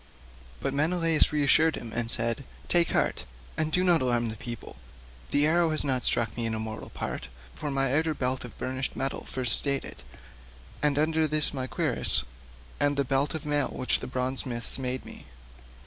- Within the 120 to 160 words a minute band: No, average, 190 wpm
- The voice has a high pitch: No, low, 135 Hz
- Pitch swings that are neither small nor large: Yes, average, 3.5 semitones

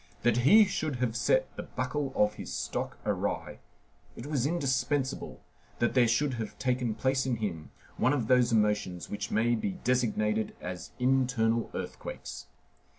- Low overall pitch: Yes, low, 125 Hz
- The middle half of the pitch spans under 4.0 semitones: Yes, average, 3.4 semitones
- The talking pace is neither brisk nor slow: Yes, average, 150 wpm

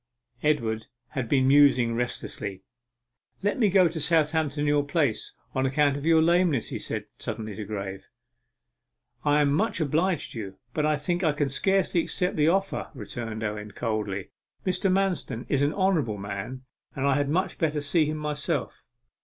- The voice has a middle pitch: Yes, medium, 145 Hz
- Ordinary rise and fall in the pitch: No, wide, 6.0 semitones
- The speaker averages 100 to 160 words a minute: No, average, 170 wpm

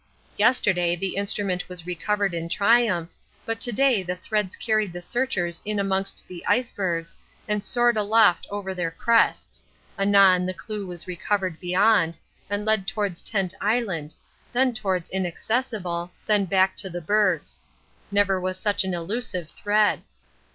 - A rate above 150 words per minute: No, average, 145 wpm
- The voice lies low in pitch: No, high, 195 Hz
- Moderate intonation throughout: Yes, average, 3.1 semitones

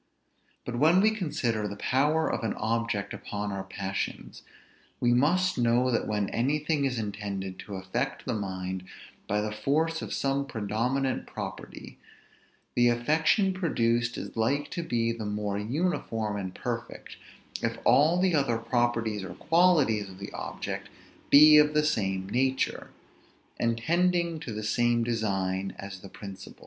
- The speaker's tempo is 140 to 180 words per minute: Yes, average, 150 wpm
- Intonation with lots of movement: Yes, wide, 6.2 semitones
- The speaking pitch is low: Yes, low, 120 Hz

